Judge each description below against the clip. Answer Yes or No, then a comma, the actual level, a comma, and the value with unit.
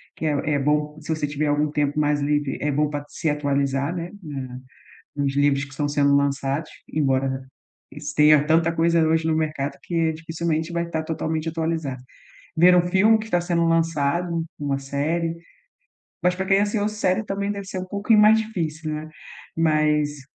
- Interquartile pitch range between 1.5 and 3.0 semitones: Yes, average, 2.7 semitones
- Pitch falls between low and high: Yes, medium, 155 Hz